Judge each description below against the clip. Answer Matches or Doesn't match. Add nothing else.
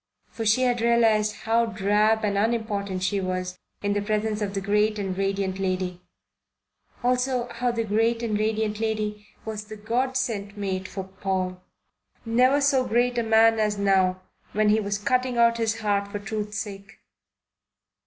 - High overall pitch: Matches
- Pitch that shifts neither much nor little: Doesn't match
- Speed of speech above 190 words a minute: Doesn't match